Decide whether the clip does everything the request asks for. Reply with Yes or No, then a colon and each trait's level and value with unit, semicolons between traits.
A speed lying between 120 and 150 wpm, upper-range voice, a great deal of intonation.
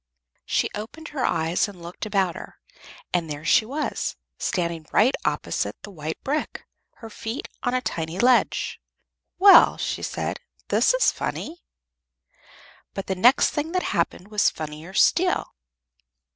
Yes: average, 145 wpm; high, 210 Hz; wide, 8.0 semitones